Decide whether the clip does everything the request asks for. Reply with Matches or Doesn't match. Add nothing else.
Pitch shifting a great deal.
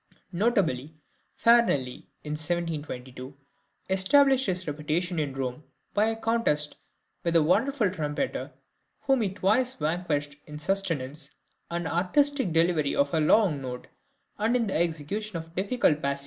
Matches